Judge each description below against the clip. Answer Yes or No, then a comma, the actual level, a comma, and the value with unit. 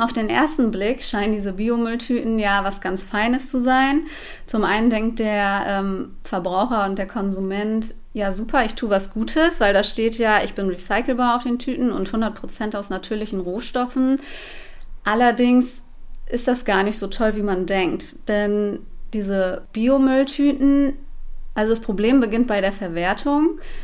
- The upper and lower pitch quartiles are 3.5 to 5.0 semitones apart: Yes, average, 3.9 semitones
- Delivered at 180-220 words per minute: No, average, 160 wpm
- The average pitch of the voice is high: Yes, high, 220 Hz